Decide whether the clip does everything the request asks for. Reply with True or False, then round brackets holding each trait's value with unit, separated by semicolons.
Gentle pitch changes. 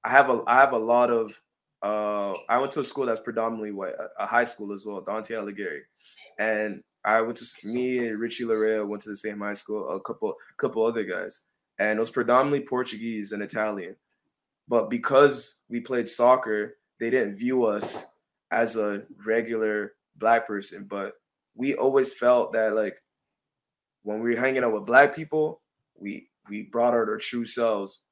True (2.3 semitones)